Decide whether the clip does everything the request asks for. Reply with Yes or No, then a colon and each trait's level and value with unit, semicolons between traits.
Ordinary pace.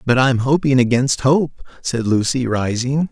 Yes: average, 175 wpm